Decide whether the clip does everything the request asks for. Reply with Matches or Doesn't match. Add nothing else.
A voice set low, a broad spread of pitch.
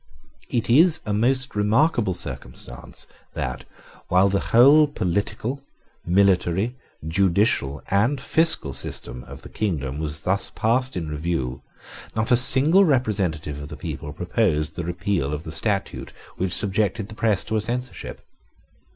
Matches